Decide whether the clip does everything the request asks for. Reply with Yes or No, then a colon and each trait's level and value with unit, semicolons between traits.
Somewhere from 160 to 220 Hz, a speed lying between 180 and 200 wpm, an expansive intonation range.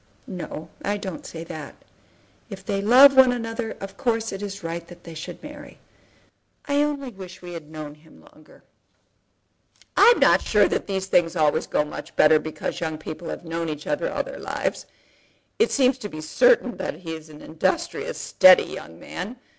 Yes: medium, 185 Hz; average, 185 wpm; wide, 7.3 semitones